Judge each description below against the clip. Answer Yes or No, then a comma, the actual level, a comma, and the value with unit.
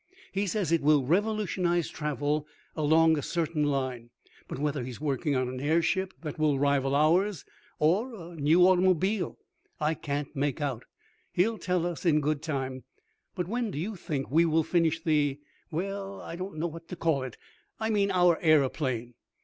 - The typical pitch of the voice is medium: Yes, medium, 160 Hz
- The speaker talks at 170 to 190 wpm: Yes, average, 175 wpm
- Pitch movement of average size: Yes, average, 3.9 semitones